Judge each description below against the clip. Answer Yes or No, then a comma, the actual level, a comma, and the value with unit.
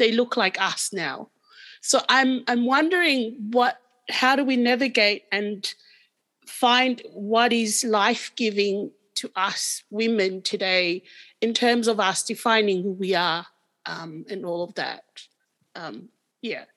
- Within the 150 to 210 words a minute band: No, slow, 135 wpm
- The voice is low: No, high, 225 Hz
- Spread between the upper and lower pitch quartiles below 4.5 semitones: Yes, average, 3.9 semitones